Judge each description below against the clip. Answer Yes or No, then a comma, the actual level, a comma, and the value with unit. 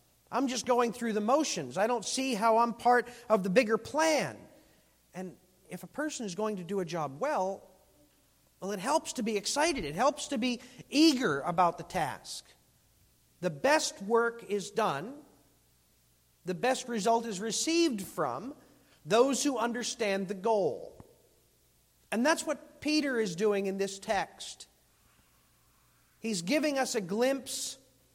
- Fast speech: No, average, 150 wpm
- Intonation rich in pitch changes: Yes, wide, 5.7 semitones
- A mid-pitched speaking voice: No, high, 230 Hz